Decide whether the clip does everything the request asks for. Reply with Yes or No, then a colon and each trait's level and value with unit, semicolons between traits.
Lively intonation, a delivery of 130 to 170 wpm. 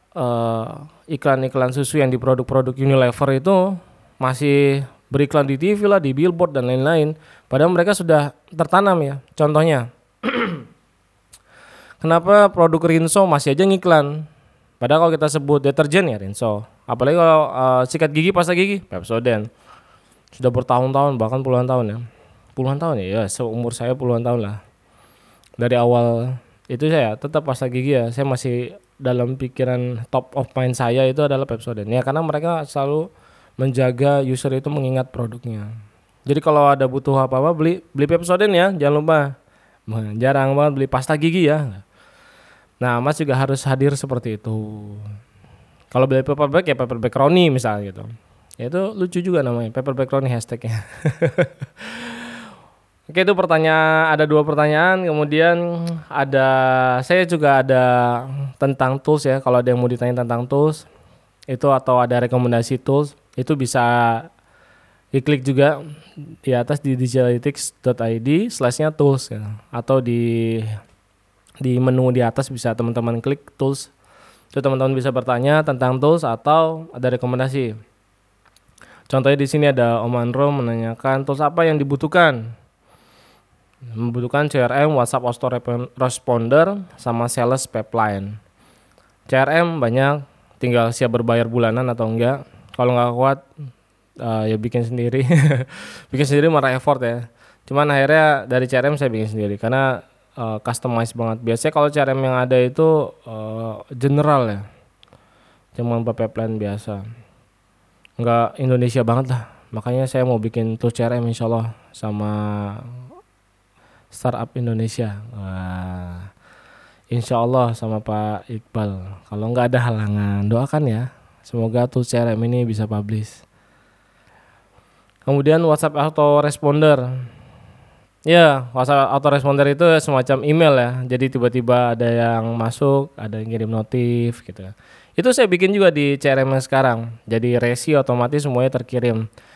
No: average, 3.7 semitones; average, 135 wpm